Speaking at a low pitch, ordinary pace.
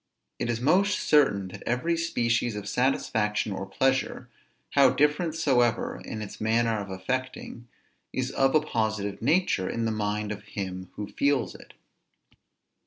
Yes: low, 120 Hz; average, 150 wpm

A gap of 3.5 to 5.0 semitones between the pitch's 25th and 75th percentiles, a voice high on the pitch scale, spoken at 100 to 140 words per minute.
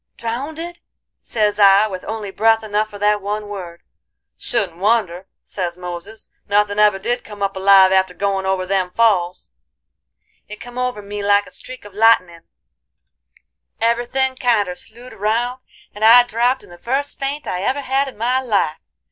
No: average, 3.8 semitones; high, 210 Hz; average, 165 wpm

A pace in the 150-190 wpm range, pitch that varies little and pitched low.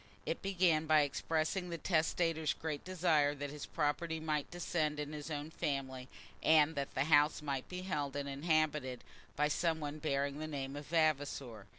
No: average, 175 wpm; narrow, 2.0 semitones; medium, 150 Hz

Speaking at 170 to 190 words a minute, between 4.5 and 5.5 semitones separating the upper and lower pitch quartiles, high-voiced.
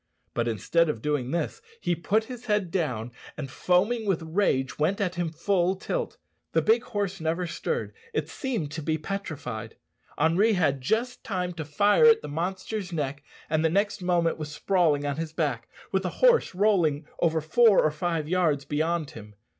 No: average, 180 wpm; average, 4.9 semitones; medium, 170 Hz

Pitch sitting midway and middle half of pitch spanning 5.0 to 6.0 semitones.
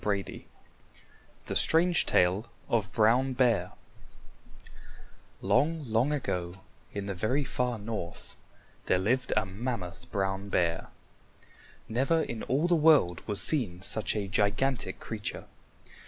No: low, 110 Hz; wide, 5.4 semitones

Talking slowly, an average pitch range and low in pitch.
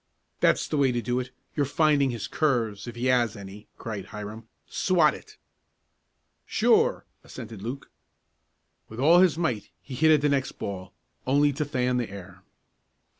No: average, 165 wpm; average, 4.7 semitones; low, 125 Hz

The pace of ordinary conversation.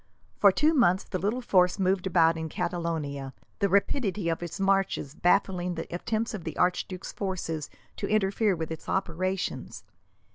Yes: average, 155 wpm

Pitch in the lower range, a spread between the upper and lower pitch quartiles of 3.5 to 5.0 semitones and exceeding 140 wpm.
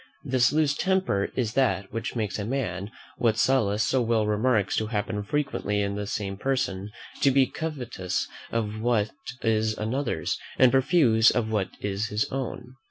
Yes: low, 110 Hz; average, 4.0 semitones; average, 165 wpm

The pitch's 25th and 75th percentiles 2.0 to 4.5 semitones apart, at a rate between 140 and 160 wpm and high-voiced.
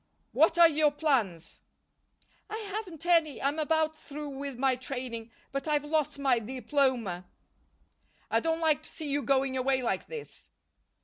Yes: average, 3.3 semitones; average, 150 wpm; very high, 285 Hz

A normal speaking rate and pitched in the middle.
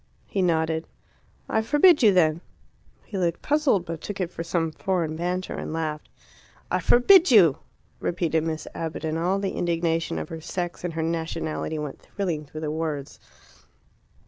Yes: average, 165 wpm; medium, 165 Hz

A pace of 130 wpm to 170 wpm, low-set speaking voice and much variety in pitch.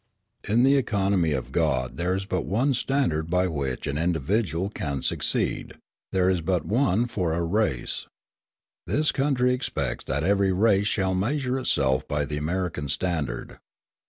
Yes: average, 155 wpm; very low, 95 Hz; wide, 5.9 semitones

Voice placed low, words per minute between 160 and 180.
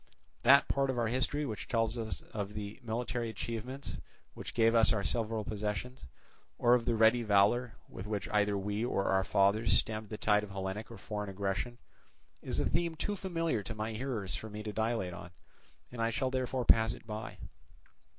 No: low, 110 Hz; average, 190 wpm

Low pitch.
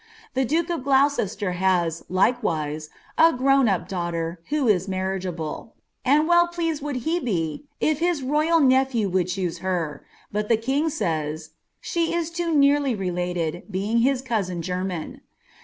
No: high, 220 Hz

